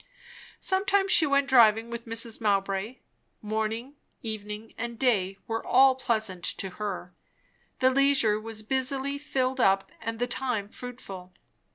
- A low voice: No, high, 225 Hz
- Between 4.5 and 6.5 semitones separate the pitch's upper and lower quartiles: No, average, 3.8 semitones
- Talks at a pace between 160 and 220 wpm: No, slow, 135 wpm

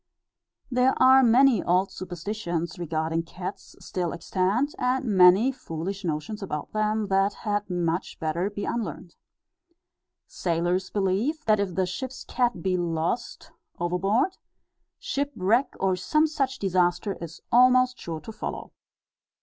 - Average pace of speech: No, slow, 125 wpm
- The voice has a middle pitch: No, high, 195 Hz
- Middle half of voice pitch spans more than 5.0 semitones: Yes, wide, 5.5 semitones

